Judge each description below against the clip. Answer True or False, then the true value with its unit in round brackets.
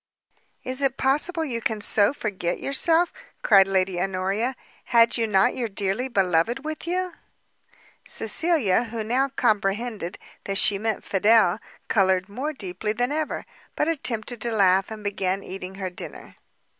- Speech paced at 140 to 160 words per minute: True (145 wpm)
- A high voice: True (220 Hz)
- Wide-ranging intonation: False (4.9 semitones)